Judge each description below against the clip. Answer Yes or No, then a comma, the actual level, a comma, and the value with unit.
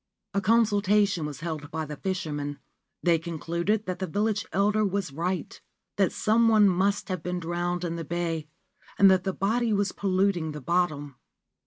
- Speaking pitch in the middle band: Yes, medium, 180 Hz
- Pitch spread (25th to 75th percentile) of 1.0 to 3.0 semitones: No, average, 3.5 semitones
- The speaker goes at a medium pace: Yes, average, 175 wpm